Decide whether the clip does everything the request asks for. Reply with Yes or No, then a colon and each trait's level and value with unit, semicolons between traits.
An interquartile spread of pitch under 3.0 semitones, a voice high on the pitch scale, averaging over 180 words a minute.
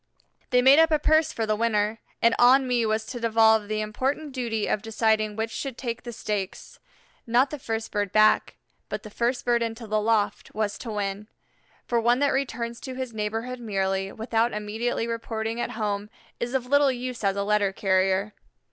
Yes: narrow, 2.5 semitones; high, 225 Hz; average, 190 wpm